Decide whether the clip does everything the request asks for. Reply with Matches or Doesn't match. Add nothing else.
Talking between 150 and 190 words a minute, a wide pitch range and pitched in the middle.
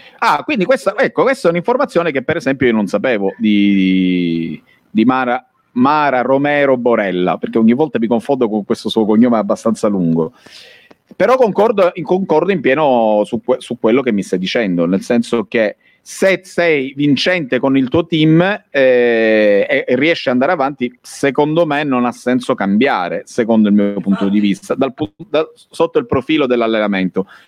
Doesn't match